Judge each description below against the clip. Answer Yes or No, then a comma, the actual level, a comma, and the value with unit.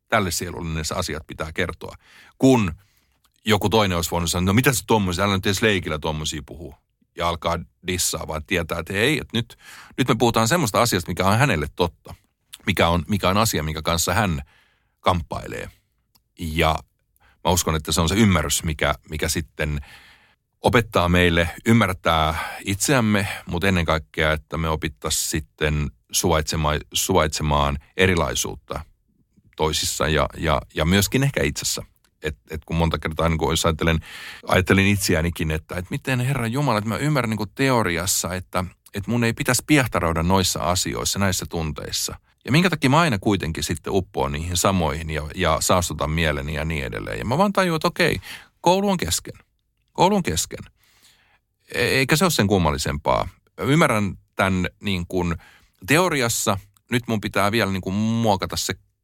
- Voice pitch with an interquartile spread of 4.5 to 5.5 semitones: Yes, average, 5.0 semitones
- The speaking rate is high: Yes, fast, 160 wpm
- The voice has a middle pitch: No, very low, 90 Hz